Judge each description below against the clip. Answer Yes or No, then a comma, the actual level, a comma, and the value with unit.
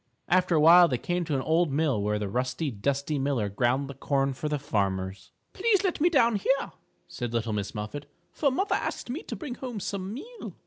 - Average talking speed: No, fast, 215 wpm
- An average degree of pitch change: No, wide, 9.0 semitones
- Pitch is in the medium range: Yes, medium, 145 Hz